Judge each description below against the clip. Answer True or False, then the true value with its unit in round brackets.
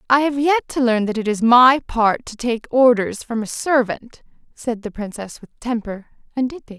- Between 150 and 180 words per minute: False (205 wpm)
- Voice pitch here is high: True (235 Hz)